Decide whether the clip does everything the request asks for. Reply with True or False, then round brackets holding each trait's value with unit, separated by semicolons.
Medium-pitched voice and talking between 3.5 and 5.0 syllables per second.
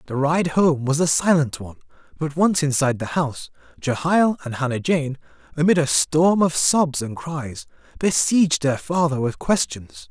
True (150 Hz; 4.8 syllables/s)